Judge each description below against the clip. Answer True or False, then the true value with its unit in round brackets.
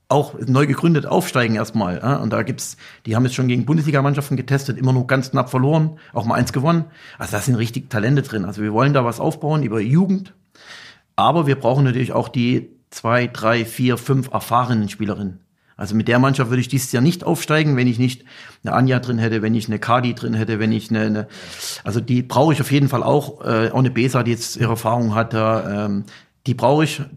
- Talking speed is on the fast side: True (220 wpm)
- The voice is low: True (125 Hz)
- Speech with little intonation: False (3.5 semitones)